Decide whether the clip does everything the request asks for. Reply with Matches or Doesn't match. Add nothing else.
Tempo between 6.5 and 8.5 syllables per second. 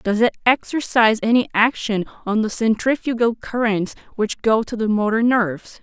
Doesn't match